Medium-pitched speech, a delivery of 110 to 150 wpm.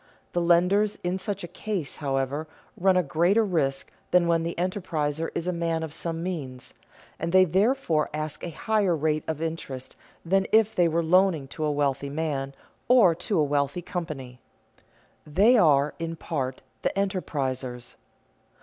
No: medium, 165 Hz; average, 160 wpm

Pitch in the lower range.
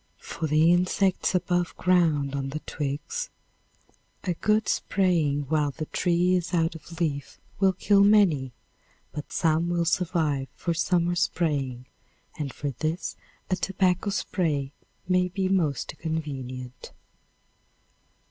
No: medium, 165 Hz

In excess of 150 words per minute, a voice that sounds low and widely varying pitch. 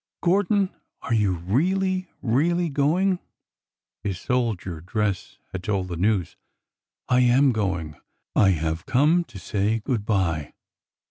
No: average, 140 wpm; low, 110 Hz; wide, 8.4 semitones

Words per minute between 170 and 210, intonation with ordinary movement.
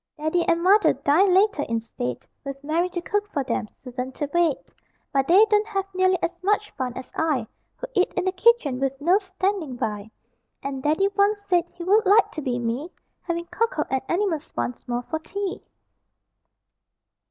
No: average, 185 wpm; wide, 6.6 semitones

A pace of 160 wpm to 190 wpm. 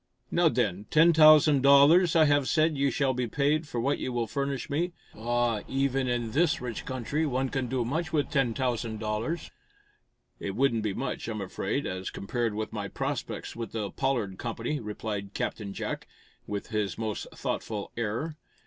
Yes: average, 175 wpm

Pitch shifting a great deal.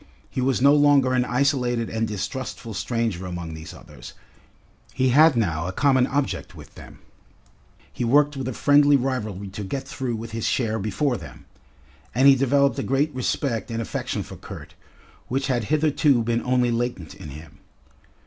No: average, 3.8 semitones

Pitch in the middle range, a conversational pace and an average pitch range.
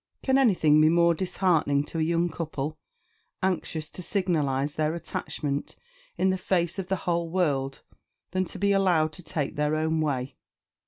Yes: medium, 165 Hz; average, 165 wpm; average, 3.3 semitones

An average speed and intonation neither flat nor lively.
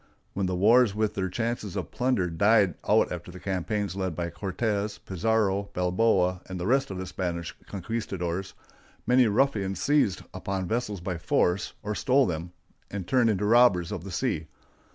Yes: average, 170 wpm; average, 3.6 semitones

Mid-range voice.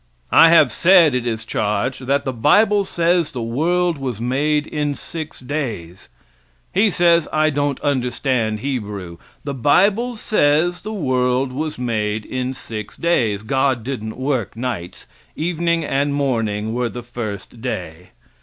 No: low, 130 Hz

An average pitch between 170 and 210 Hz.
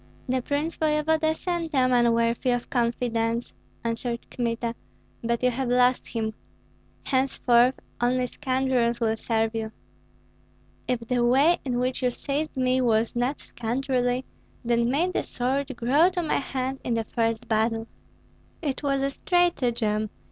No: very high, 250 Hz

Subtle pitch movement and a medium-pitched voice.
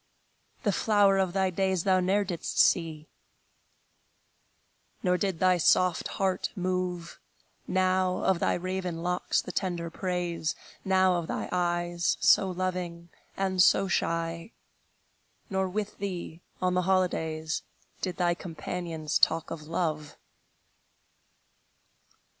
Yes: narrow, 1.7 semitones; medium, 180 Hz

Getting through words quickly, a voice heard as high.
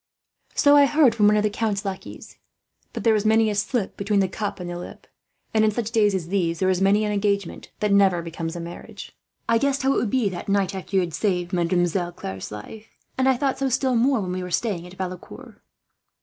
Yes: fast, 235 wpm; high, 200 Hz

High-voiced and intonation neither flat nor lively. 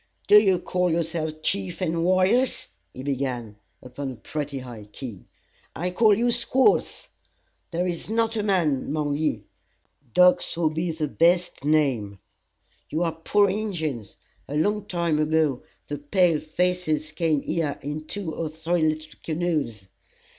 No: medium, 160 Hz; average, 3.7 semitones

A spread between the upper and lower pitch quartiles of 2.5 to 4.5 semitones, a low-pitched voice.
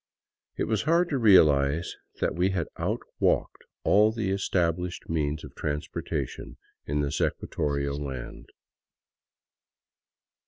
No: average, 5.3 semitones; very low, 85 Hz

